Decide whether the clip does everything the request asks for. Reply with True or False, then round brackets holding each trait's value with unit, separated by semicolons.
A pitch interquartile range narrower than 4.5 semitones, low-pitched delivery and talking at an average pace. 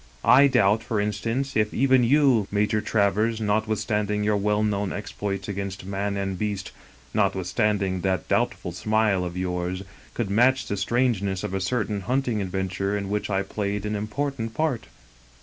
True (2.4 semitones; 105 Hz; 160 wpm)